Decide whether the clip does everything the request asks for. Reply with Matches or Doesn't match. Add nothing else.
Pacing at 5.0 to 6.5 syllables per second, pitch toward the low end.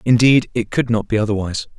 Matches